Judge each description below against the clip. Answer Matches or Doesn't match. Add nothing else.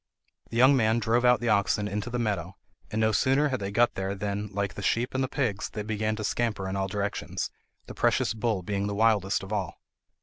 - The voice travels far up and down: Doesn't match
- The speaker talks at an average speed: Doesn't match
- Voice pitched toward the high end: Doesn't match